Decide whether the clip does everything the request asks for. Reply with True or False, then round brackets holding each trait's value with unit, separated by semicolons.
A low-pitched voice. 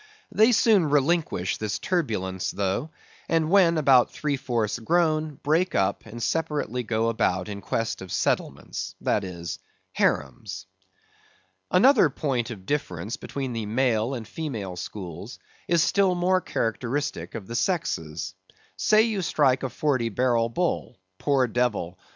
True (125 Hz)